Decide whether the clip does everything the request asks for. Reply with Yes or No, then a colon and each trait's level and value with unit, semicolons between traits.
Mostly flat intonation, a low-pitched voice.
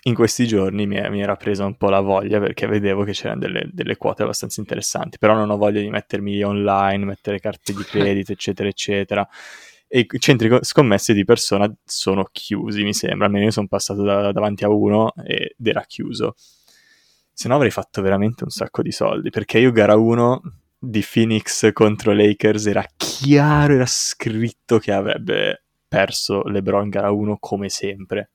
Yes: narrow, 1.6 semitones; low, 105 Hz